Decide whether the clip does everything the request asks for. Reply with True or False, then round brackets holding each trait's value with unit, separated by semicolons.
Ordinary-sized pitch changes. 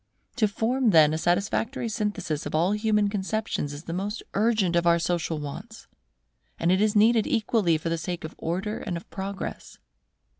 True (4.3 semitones)